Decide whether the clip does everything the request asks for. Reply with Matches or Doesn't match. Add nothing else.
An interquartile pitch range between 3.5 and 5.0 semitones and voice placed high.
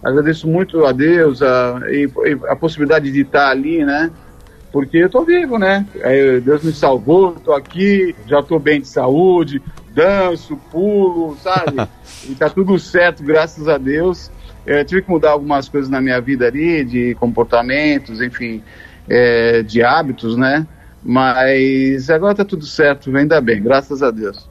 Doesn't match